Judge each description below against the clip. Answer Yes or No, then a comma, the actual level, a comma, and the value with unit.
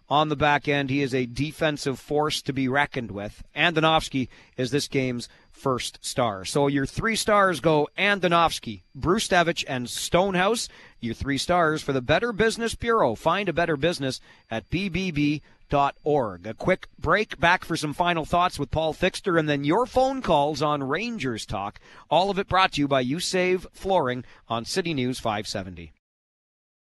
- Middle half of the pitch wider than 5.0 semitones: Yes, wide, 5.4 semitones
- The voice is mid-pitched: Yes, medium, 150 Hz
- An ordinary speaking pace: Yes, average, 170 wpm